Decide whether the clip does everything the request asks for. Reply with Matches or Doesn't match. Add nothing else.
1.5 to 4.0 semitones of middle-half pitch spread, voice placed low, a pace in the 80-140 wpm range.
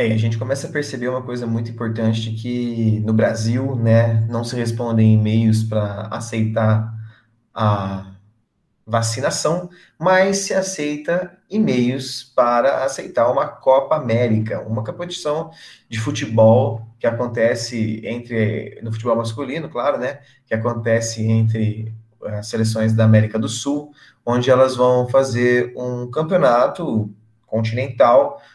Matches